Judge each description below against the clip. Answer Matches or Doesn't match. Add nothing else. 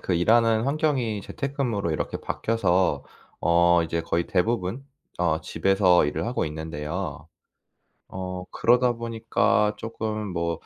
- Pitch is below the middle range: Matches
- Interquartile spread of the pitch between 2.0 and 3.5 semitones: Doesn't match